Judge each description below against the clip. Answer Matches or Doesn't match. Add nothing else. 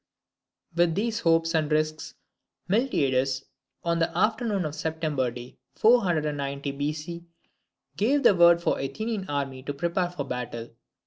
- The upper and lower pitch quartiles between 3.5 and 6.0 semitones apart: Matches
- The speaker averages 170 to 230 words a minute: Doesn't match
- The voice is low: Doesn't match